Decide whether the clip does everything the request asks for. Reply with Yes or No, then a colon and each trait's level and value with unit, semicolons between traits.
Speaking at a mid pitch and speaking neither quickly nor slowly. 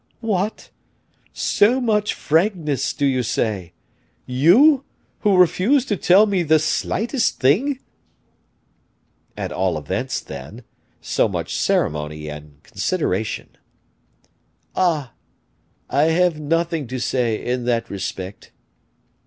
No: medium, 150 Hz; slow, 105 wpm